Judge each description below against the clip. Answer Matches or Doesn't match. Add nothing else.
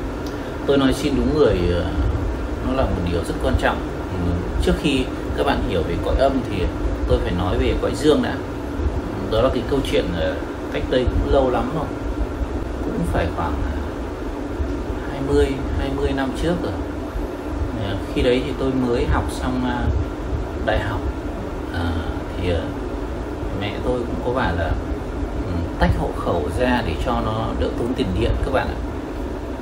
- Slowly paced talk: Doesn't match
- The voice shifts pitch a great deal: Matches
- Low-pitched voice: Matches